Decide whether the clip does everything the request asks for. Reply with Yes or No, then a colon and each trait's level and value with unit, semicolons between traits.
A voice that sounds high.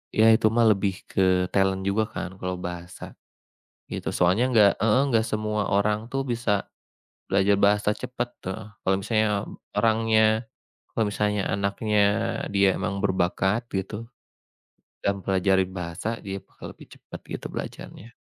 No: low, 105 Hz